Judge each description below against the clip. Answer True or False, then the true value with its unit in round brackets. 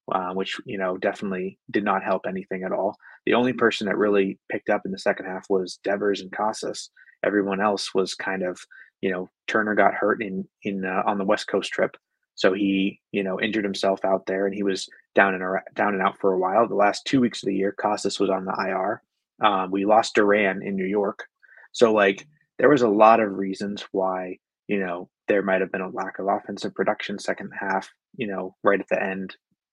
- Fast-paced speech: True (220 wpm)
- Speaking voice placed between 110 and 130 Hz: False (95 Hz)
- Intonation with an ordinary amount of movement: False (1.3 semitones)